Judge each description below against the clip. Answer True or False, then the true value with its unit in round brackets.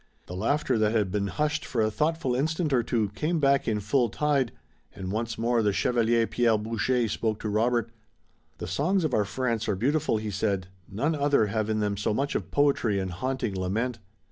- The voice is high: False (115 Hz)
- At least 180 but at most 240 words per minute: True (200 wpm)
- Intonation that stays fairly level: False (4.5 semitones)